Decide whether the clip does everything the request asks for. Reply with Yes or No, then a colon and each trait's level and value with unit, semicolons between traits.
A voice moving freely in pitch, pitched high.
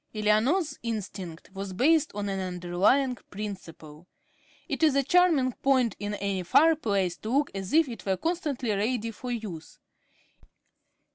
Yes: wide, 6.2 semitones; high, 215 Hz